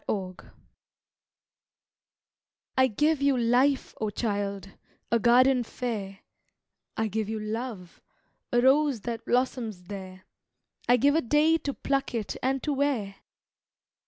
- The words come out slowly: Yes, slow, 130 wpm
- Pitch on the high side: Yes, high, 235 Hz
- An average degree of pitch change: Yes, average, 4.6 semitones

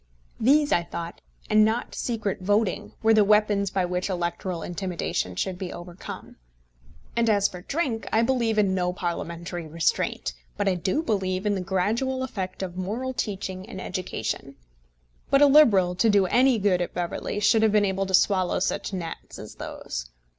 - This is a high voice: Yes, high, 195 Hz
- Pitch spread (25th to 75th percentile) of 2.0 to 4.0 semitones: Yes, average, 3.5 semitones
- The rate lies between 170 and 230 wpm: Yes, average, 175 wpm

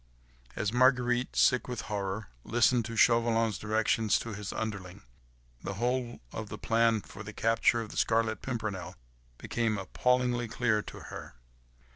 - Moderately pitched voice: No, low, 115 Hz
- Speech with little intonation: Yes, narrow, 2.3 semitones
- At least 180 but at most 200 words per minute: No, average, 145 wpm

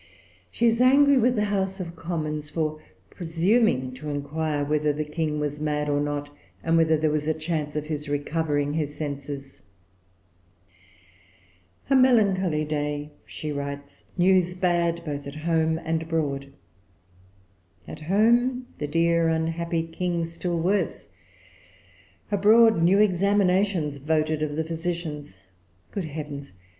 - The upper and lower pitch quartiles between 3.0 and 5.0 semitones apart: Yes, average, 3.4 semitones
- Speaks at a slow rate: Yes, slow, 130 wpm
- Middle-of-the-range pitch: Yes, medium, 160 Hz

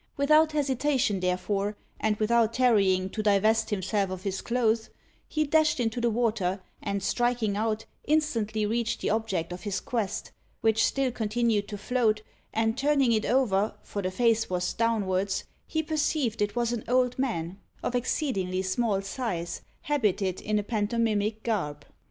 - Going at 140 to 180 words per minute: Yes, average, 155 wpm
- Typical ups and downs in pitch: Yes, average, 3.4 semitones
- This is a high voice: Yes, high, 220 Hz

